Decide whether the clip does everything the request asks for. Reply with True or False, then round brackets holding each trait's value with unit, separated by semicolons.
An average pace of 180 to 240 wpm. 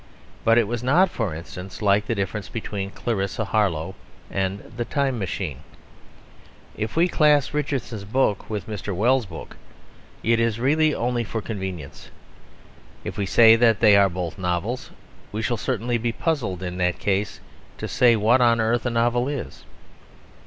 False (160 wpm)